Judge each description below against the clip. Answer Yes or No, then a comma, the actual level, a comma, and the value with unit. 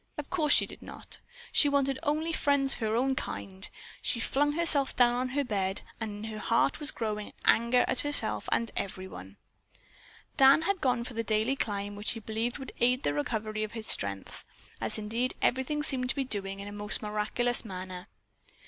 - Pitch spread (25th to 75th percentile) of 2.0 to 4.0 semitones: No, average, 4.4 semitones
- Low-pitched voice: No, high, 235 Hz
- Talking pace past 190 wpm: Yes, average, 200 wpm